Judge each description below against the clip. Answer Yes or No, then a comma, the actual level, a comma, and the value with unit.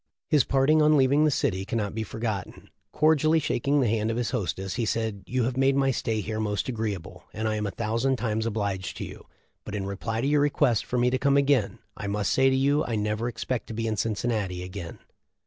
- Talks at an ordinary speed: No, fast, 230 wpm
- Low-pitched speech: Yes, low, 115 Hz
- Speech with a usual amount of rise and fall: Yes, average, 4.1 semitones